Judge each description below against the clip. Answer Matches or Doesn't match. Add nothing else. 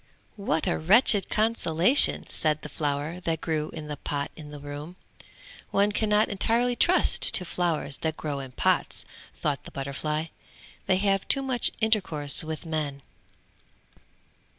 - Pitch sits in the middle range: Matches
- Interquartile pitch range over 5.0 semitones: Matches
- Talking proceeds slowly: Doesn't match